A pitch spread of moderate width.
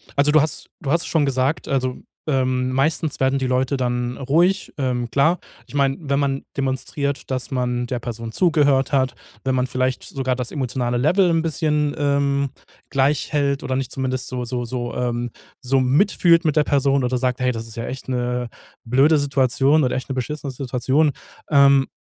No: narrow, 2.1 semitones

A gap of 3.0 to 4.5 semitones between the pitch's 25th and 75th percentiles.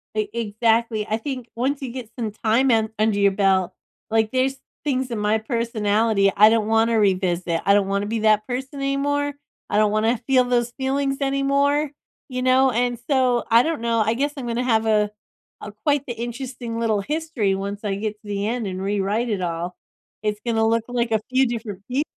Yes: average, 3.5 semitones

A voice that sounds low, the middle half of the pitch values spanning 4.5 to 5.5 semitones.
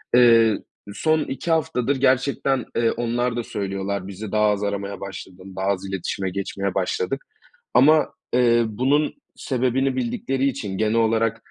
Yes: low, 115 Hz; average, 4.8 semitones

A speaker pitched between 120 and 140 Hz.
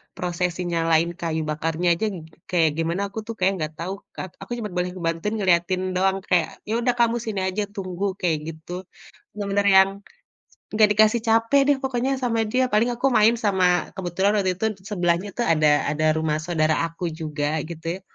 No: medium, 185 Hz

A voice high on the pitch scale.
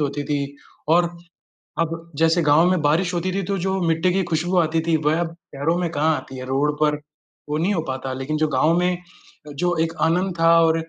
No: medium, 165 Hz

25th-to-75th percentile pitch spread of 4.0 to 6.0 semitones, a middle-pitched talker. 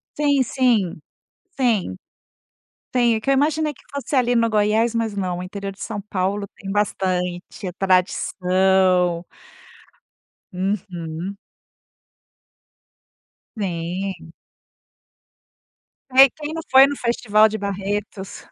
No: average, 4.4 semitones; high, 200 Hz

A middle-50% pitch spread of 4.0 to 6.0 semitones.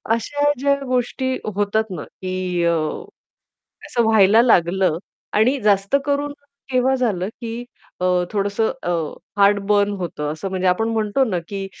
Yes: average, 4.6 semitones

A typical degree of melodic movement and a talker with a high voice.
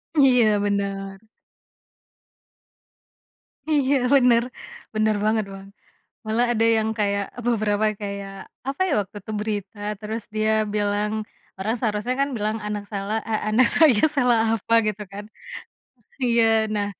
No: narrow, 2.2 semitones; high, 215 Hz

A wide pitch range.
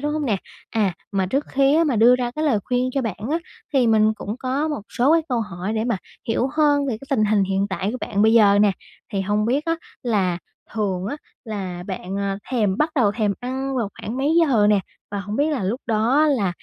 No: average, 4.9 semitones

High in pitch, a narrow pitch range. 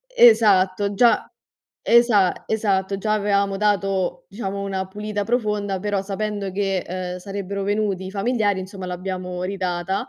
Yes: high, 195 Hz; narrow, 1.8 semitones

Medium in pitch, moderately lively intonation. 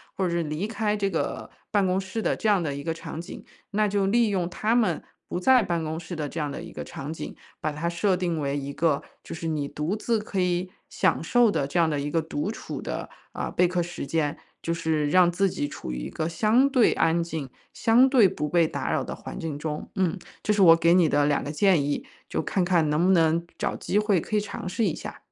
Yes: medium, 170 Hz; average, 4.2 semitones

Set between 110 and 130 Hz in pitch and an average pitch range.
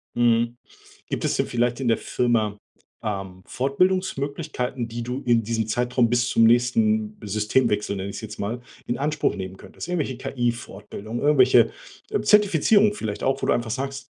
Yes: low, 120 Hz; average, 3.5 semitones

